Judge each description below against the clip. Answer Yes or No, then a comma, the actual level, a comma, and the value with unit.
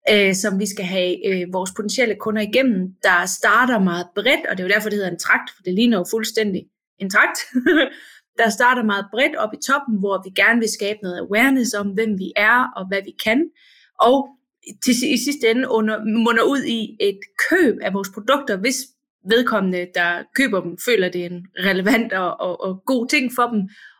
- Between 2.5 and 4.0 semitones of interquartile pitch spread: No, average, 4.6 semitones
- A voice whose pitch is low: No, high, 220 Hz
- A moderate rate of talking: Yes, average, 200 wpm